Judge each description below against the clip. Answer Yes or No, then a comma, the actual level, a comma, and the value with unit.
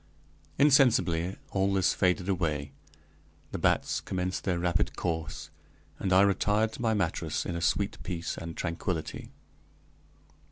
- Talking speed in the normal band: No, slow, 125 wpm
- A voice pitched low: Yes, very low, 90 Hz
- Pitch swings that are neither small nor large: Yes, average, 3.1 semitones